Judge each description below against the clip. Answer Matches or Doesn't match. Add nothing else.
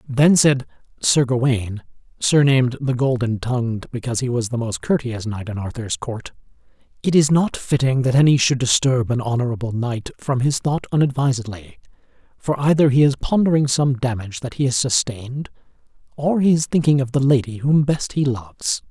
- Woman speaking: Doesn't match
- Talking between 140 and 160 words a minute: Doesn't match